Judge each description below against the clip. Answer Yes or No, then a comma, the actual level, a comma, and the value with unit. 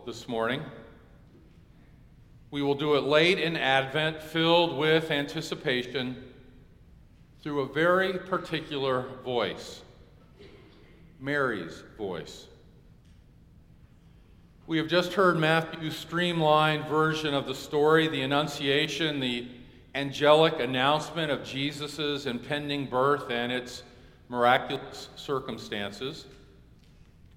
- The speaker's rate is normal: No, slow, 90 wpm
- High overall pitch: No, medium, 145 Hz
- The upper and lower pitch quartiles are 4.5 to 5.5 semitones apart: No, average, 3.6 semitones